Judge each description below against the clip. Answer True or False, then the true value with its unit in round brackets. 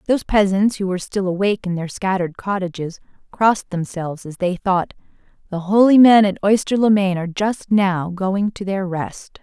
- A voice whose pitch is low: False (195 Hz)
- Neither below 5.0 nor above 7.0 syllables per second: True (5.3 syllables/s)